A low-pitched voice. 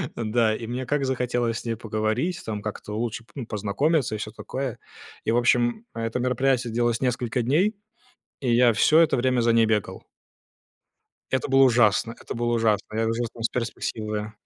Yes: low, 120 Hz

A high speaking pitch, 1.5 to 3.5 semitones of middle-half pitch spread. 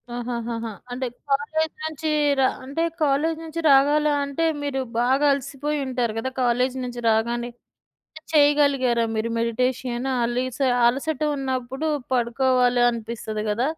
Yes: very high, 255 Hz; average, 3.2 semitones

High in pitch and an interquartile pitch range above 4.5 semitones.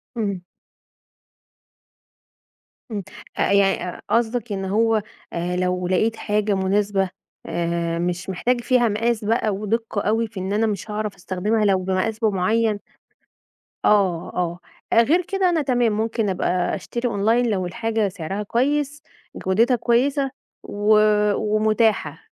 No: high, 210 Hz; average, 3.3 semitones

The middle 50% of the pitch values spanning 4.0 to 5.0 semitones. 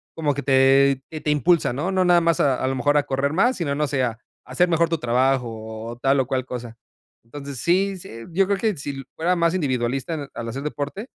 Yes: average, 4.5 semitones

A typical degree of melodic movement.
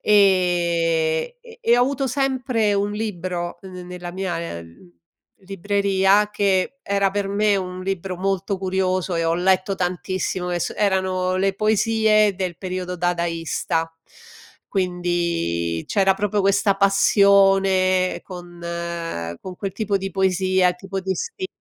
No: narrow, 2.0 semitones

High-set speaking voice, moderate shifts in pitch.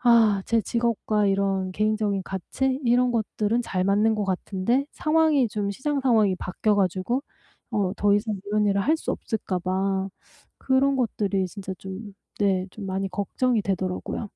Yes: high, 205 Hz; average, 3.4 semitones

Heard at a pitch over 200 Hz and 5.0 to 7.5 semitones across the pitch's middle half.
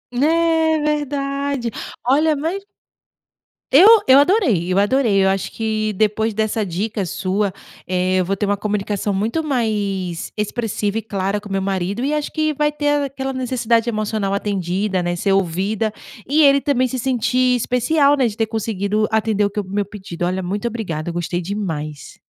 Yes: high, 215 Hz; wide, 5.4 semitones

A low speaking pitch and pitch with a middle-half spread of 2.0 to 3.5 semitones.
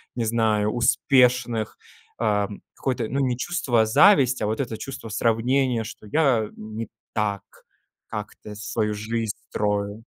Yes: low, 115 Hz; average, 2.7 semitones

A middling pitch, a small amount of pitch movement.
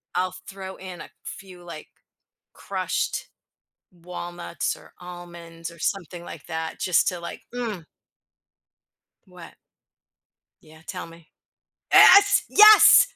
Yes: medium, 175 Hz; narrow, 2.1 semitones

